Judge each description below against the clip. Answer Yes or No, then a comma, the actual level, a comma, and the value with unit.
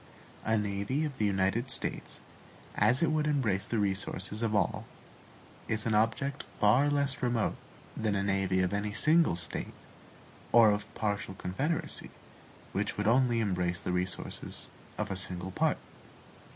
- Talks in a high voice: No, low, 105 Hz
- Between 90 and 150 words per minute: Yes, average, 145 wpm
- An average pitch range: Yes, average, 4.4 semitones